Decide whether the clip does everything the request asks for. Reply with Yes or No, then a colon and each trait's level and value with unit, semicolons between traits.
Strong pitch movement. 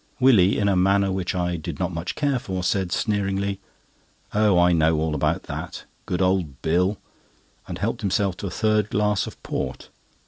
No: narrow, 2.6 semitones